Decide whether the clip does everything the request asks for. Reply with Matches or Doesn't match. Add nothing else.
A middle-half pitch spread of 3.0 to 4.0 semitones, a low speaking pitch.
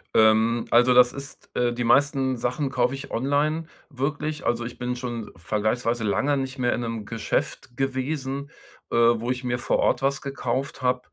Doesn't match